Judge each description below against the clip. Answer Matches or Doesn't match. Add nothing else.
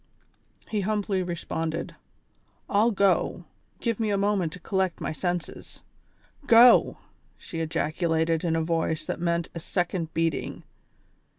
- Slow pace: Matches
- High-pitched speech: Doesn't match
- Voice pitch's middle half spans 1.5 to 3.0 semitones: Doesn't match